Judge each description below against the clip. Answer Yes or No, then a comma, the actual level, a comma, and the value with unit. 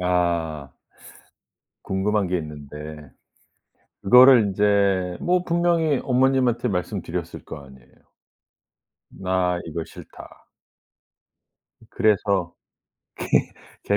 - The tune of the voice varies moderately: No, wide, 6.3 semitones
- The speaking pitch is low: Yes, very low, 95 Hz